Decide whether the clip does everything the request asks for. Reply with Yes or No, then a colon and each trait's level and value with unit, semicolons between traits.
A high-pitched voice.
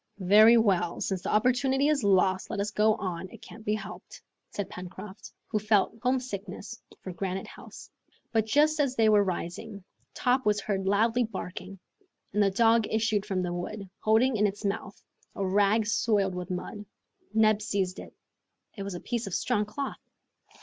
Yes: high, 210 Hz